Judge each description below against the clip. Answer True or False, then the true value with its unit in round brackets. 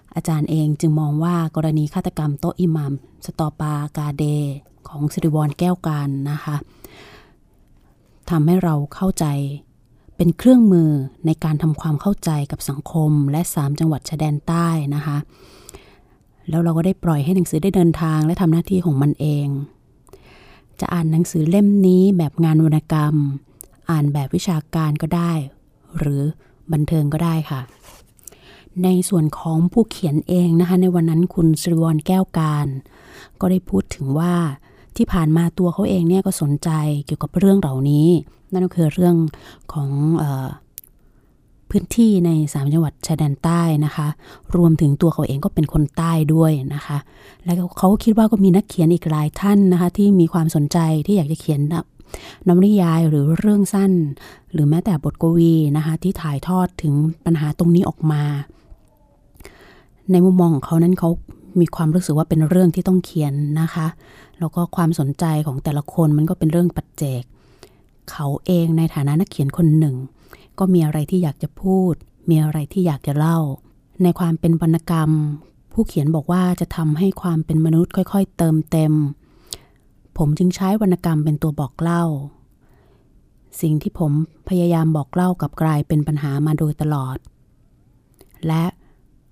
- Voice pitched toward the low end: False (160 Hz)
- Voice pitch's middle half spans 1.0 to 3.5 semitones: True (2.7 semitones)